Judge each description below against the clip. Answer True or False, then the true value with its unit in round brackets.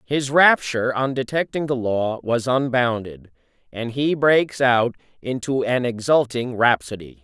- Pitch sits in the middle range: False (125 Hz)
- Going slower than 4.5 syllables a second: True (4.2 syllables/s)